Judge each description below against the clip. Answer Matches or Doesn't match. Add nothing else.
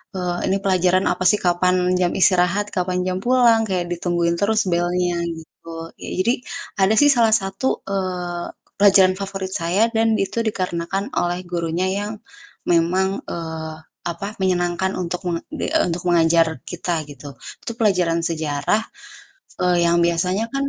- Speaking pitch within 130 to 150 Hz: Doesn't match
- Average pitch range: Doesn't match